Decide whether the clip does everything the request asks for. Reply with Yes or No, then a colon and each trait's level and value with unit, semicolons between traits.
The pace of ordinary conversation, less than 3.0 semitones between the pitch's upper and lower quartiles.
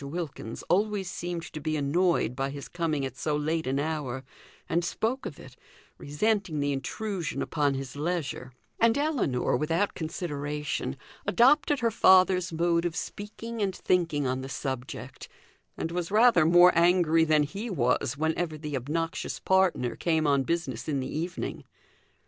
No: average, 155 wpm; average, 4.3 semitones